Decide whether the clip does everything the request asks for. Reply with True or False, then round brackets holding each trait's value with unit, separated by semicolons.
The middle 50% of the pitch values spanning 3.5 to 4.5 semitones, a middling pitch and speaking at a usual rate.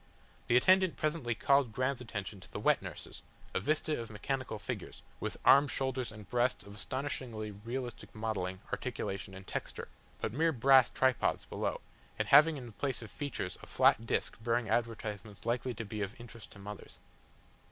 False (4.0 semitones; 120 Hz; 175 wpm)